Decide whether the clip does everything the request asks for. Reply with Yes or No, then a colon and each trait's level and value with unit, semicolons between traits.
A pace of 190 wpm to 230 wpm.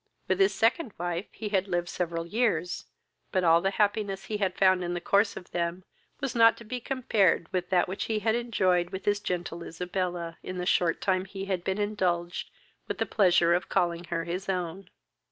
Yes: fast, 205 wpm